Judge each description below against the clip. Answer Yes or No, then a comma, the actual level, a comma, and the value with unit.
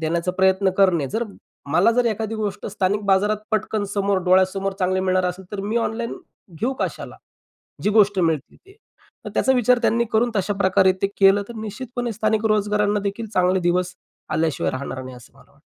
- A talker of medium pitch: No, high, 200 Hz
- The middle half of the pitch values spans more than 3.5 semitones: No, average, 2.9 semitones